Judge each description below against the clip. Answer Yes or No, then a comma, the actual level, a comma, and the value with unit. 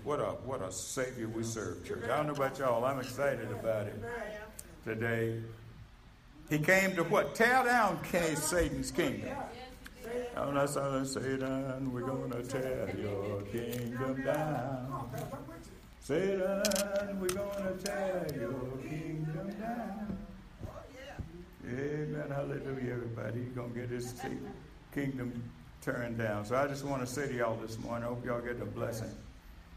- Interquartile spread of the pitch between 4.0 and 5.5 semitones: Yes, average, 4.5 semitones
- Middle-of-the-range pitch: No, low, 130 Hz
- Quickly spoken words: No, average, 145 wpm